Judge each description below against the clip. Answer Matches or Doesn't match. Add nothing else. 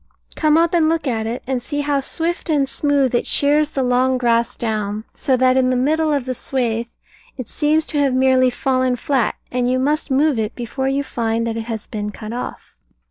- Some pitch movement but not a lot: Matches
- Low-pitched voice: Doesn't match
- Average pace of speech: Doesn't match